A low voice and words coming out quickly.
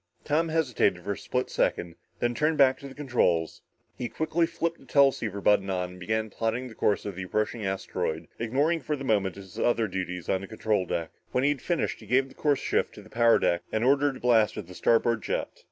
Yes: low, 115 Hz; fast, 230 wpm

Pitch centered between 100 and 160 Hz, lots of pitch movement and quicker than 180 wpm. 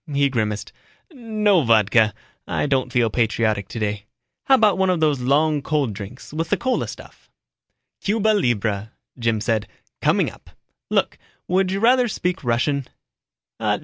No: low, 135 Hz; wide, 9.0 semitones; average, 145 wpm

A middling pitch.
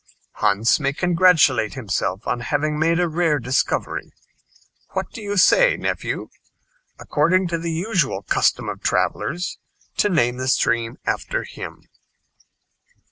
Yes: medium, 155 Hz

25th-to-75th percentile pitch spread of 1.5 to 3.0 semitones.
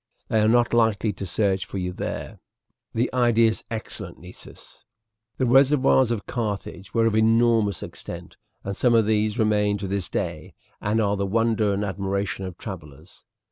Yes: average, 2.7 semitones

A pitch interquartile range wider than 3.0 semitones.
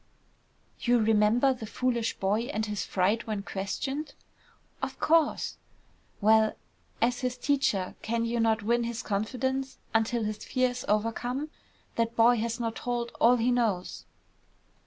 No: narrow, 2.4 semitones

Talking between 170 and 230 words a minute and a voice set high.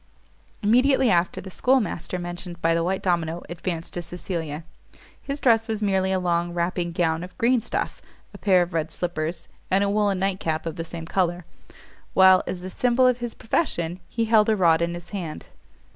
No: average, 190 wpm; medium, 180 Hz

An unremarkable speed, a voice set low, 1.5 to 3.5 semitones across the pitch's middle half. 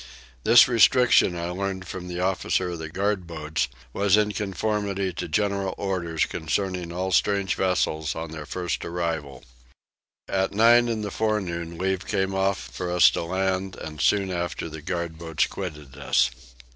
Yes: average, 160 wpm; very low, 90 Hz; average, 2.8 semitones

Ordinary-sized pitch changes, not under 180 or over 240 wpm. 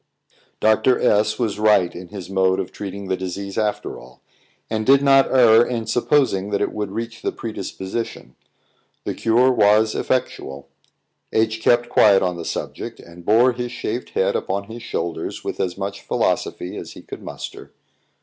No: average, 3.7 semitones; average, 170 wpm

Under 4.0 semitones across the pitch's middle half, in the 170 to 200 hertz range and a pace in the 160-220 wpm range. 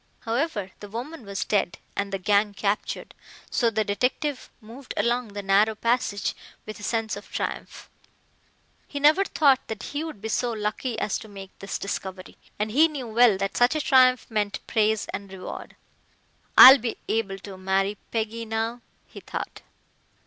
No: average, 3.5 semitones; high, 220 Hz; average, 170 wpm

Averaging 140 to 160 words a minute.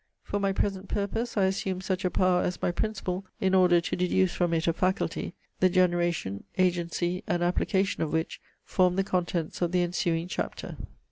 No: average, 185 wpm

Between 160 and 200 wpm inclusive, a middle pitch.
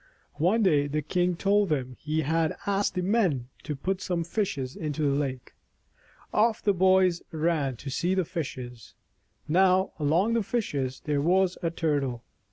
Yes: average, 170 wpm; medium, 165 Hz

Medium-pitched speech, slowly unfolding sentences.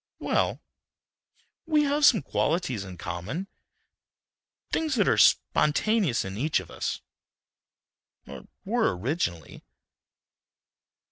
Yes: medium, 150 Hz; slow, 90 wpm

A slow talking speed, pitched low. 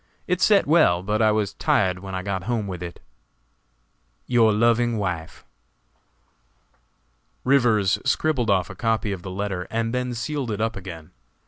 No: average, 155 wpm; low, 110 Hz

